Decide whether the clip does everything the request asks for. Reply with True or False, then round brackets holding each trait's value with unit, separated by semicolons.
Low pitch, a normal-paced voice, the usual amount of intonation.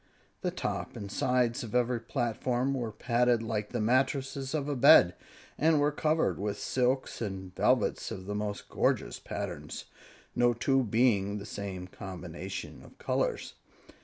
True (120 Hz; 155 wpm; 4.3 semitones)